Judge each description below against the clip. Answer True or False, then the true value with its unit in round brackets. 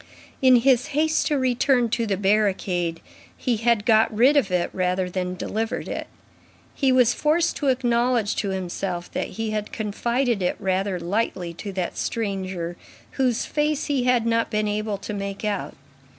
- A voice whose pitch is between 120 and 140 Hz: False (215 Hz)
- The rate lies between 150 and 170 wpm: True (165 wpm)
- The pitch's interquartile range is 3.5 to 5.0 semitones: True (4.5 semitones)